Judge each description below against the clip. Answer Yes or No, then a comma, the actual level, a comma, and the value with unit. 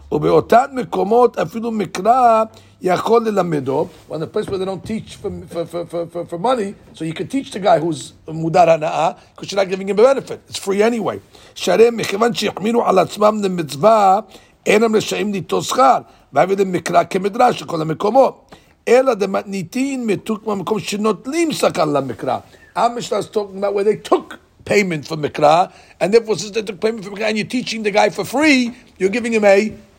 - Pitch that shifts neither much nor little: Yes, average, 3.5 semitones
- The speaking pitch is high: Yes, high, 205 Hz